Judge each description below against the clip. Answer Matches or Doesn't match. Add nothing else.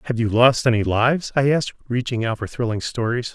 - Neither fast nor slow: Doesn't match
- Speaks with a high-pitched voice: Doesn't match